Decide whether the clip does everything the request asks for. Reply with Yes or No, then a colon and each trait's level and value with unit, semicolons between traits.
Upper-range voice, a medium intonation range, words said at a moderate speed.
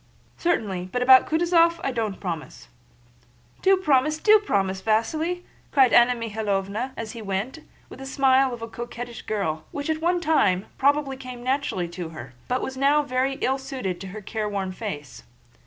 No: high, 245 Hz; wide, 5.8 semitones; average, 170 wpm